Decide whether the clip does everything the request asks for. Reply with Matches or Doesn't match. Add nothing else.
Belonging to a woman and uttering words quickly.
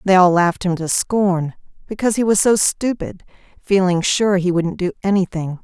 Doesn't match